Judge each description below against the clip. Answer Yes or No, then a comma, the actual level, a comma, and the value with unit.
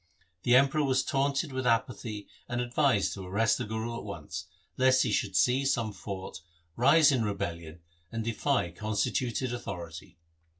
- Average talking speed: Yes, average, 155 wpm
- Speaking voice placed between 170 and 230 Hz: No, low, 115 Hz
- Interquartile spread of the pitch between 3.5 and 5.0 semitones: Yes, average, 4.7 semitones